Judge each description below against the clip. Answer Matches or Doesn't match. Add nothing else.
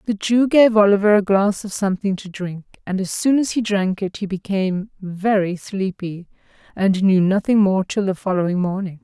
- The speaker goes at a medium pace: Matches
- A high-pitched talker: Matches